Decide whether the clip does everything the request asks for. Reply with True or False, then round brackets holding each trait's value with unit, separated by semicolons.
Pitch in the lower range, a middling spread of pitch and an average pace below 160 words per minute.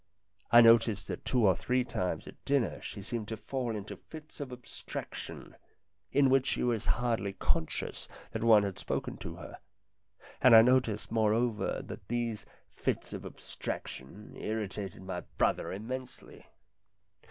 True (115 Hz; 3.2 semitones; 145 wpm)